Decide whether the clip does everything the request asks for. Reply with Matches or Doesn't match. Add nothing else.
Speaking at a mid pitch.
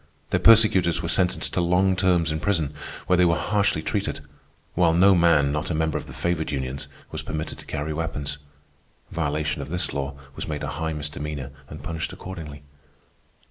Doesn't match